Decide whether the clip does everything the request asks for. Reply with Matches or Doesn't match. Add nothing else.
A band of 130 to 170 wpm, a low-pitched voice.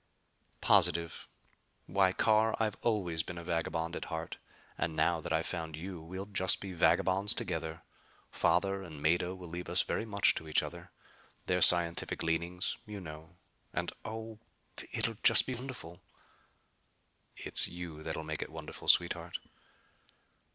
Matches